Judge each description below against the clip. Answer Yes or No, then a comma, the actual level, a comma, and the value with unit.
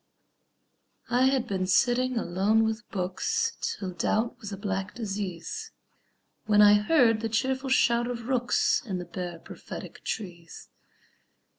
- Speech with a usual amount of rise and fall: Yes, average, 4.3 semitones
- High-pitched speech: Yes, high, 220 Hz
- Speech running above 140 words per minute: No, slow, 135 wpm